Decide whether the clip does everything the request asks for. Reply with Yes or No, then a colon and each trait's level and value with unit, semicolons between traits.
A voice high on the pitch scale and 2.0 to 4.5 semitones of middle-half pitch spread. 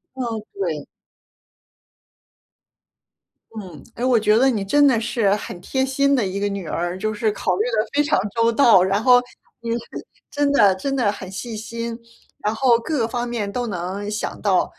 Yes: high, 225 Hz; average, 3.8 semitones